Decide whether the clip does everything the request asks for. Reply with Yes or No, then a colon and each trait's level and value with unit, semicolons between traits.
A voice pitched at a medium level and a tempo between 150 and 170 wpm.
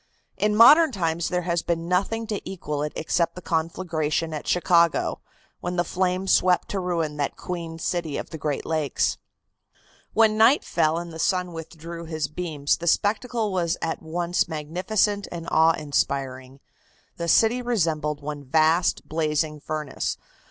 Yes: medium, 170 Hz; average, 160 wpm